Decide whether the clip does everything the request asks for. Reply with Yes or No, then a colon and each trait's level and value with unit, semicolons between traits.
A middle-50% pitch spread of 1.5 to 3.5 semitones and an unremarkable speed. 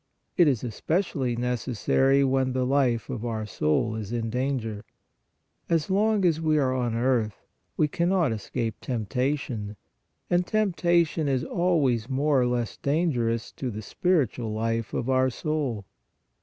No: average, 4.9 semitones; average, 150 wpm